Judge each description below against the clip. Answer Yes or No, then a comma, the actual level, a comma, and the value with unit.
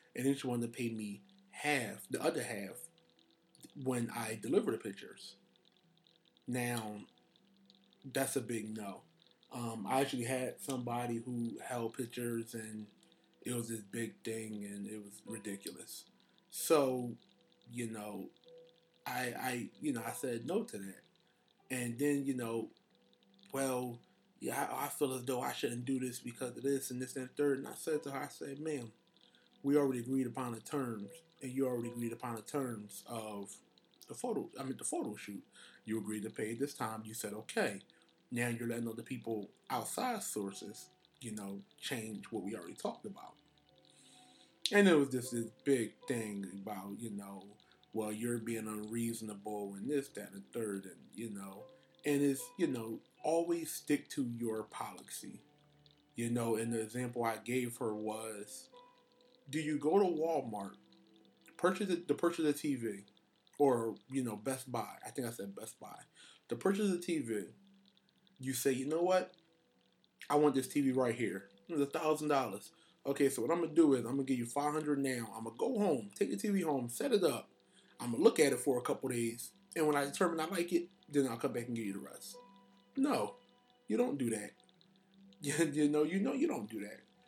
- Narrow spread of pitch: No, average, 4.9 semitones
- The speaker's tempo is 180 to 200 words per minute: Yes, average, 185 wpm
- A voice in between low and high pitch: No, low, 125 Hz